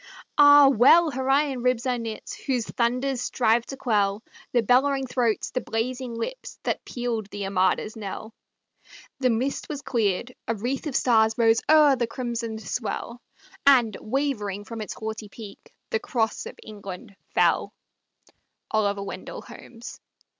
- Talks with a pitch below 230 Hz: No, high, 235 Hz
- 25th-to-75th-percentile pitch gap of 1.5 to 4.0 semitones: Yes, average, 3.2 semitones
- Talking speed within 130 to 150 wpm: Yes, average, 140 wpm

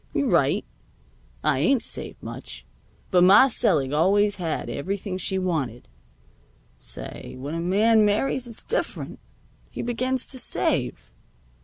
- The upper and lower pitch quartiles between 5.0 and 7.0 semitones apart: Yes, wide, 5.6 semitones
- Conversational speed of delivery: No, slow, 130 wpm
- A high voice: Yes, high, 195 Hz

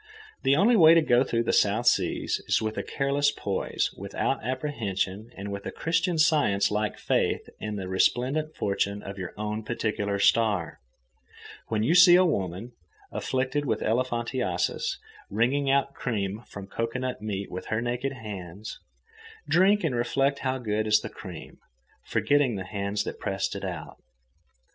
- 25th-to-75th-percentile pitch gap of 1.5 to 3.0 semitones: No, average, 5.2 semitones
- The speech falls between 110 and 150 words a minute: No, average, 160 wpm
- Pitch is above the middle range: No, low, 115 Hz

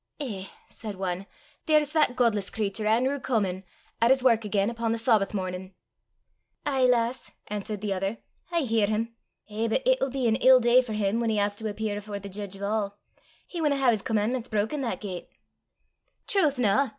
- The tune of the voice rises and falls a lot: No, average, 3.8 semitones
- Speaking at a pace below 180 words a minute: No, average, 190 wpm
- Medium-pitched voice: No, high, 220 Hz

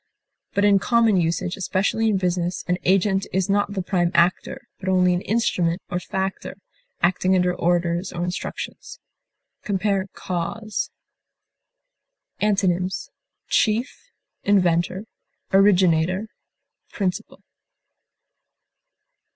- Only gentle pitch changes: Yes, narrow, 2.1 semitones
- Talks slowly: Yes, slow, 100 wpm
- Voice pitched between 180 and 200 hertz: Yes, medium, 185 Hz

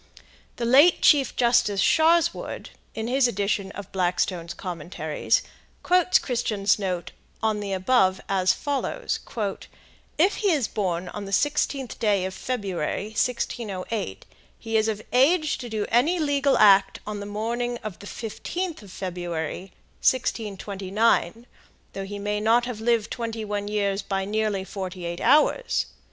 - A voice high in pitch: Yes, high, 210 Hz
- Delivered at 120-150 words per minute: Yes, average, 140 wpm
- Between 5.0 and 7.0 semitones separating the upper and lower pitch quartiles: No, average, 4.2 semitones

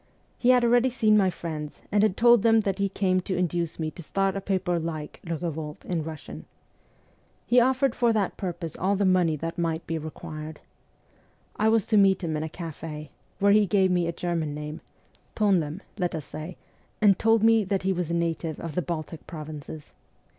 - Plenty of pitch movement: No, average, 4.1 semitones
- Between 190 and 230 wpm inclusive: Yes, fast, 205 wpm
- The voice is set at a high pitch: No, medium, 175 Hz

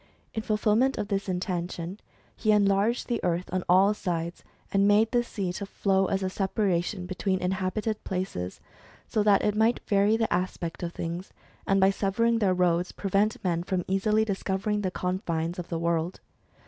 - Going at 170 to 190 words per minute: Yes, average, 175 wpm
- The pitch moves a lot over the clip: No, average, 2.7 semitones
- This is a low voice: No, high, 195 Hz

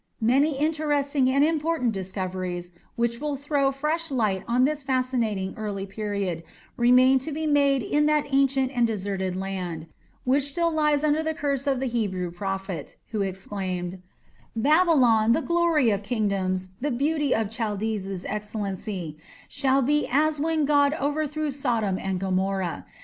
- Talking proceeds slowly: No, average, 150 wpm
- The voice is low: No, high, 245 Hz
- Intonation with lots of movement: Yes, wide, 6.9 semitones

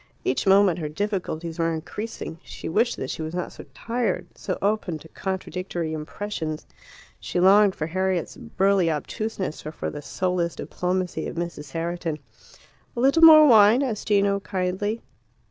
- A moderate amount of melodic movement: Yes, average, 3.9 semitones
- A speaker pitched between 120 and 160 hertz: No, medium, 185 Hz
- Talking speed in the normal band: Yes, average, 155 wpm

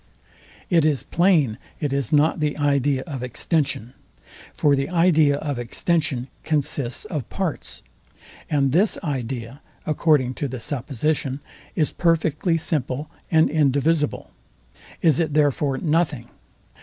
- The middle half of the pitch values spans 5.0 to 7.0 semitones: No, average, 3.0 semitones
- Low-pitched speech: No, medium, 145 Hz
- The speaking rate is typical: No, slow, 120 wpm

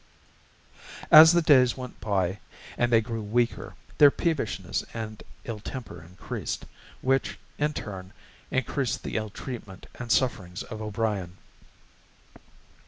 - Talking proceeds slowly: Yes, slow, 120 wpm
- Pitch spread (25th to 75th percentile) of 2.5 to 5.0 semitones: Yes, average, 4.1 semitones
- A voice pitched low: Yes, low, 115 Hz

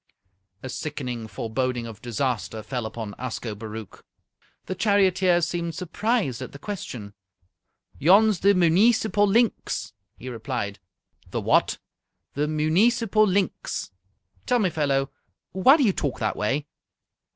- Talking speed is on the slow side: Yes, slow, 120 wpm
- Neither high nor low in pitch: Yes, medium, 155 Hz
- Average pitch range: No, wide, 8.7 semitones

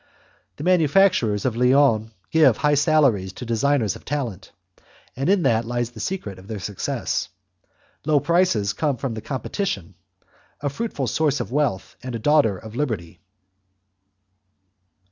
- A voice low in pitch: Yes, low, 125 Hz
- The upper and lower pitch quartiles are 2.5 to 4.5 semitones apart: No, average, 5.3 semitones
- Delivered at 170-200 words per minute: No, slow, 135 wpm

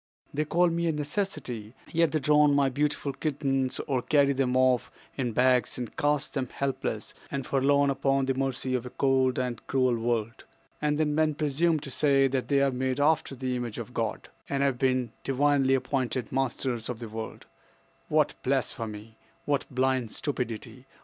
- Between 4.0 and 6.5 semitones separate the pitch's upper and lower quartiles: No, narrow, 2.4 semitones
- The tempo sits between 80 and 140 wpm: No, average, 175 wpm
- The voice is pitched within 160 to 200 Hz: No, low, 135 Hz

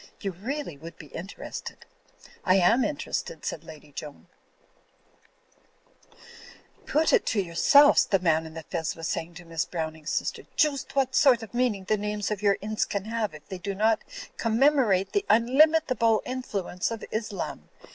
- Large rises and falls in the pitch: Yes, wide, 6.8 semitones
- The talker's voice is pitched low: No, high, 210 Hz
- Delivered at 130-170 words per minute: Yes, average, 165 wpm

